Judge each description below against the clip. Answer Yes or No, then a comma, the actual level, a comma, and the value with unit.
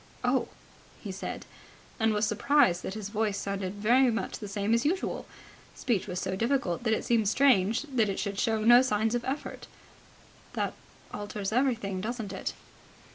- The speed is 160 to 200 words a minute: Yes, average, 170 wpm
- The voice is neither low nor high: No, high, 220 Hz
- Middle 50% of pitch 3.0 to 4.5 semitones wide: Yes, average, 3.3 semitones